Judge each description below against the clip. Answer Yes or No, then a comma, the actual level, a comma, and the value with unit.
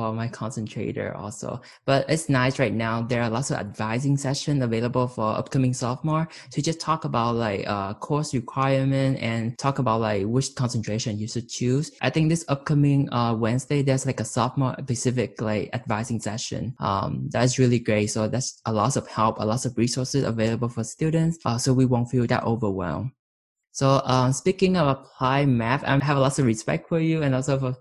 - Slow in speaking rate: No, average, 195 wpm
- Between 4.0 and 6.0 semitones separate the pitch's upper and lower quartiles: No, average, 3.2 semitones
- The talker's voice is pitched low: Yes, low, 125 Hz